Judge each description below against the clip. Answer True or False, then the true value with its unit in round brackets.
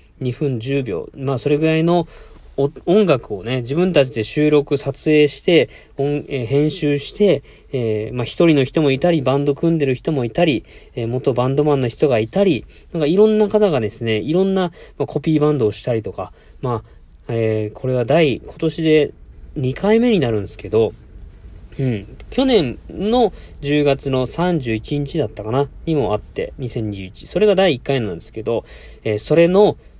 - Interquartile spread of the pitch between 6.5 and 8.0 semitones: False (5.3 semitones)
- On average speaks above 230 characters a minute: True (280 characters per minute)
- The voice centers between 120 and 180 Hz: True (140 Hz)